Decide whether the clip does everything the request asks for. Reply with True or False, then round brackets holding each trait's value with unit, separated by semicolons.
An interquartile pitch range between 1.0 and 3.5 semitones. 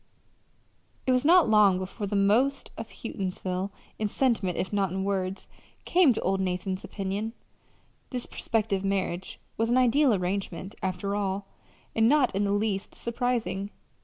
True (3.2 semitones)